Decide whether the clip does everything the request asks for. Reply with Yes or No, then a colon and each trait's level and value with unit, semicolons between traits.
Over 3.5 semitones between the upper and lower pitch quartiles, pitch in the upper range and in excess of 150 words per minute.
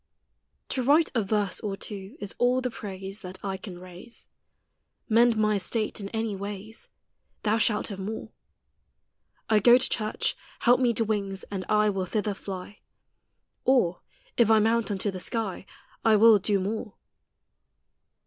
No: narrow, 2.6 semitones; high, 210 Hz; average, 160 wpm